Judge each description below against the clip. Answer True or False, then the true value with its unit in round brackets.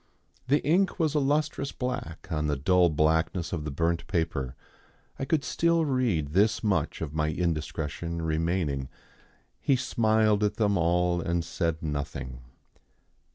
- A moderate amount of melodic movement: False (6.5 semitones)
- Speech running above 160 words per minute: False (145 wpm)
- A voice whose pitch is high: False (85 Hz)